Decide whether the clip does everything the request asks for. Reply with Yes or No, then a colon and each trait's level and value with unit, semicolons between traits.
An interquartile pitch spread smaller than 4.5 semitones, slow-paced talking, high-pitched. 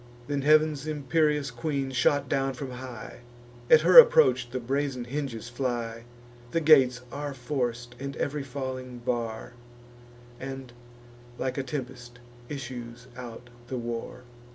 No: narrow, 2.6 semitones; slow, 130 wpm; low, 130 Hz